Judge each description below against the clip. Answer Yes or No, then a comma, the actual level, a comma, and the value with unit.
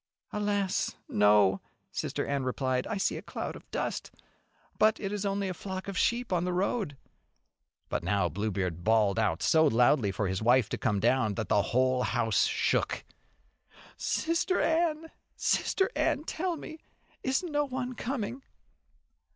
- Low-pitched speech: No, medium, 160 Hz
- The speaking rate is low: No, average, 155 wpm